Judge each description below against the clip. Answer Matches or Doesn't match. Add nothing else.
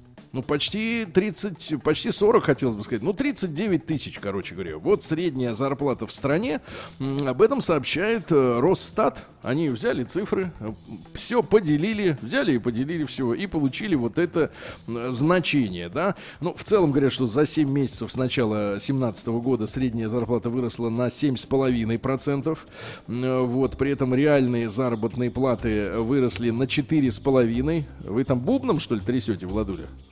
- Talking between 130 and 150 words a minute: Matches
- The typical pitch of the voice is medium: Doesn't match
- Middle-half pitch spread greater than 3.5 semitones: Matches